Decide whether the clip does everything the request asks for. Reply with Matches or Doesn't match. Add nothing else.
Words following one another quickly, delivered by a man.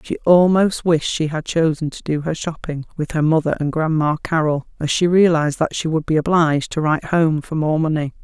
Doesn't match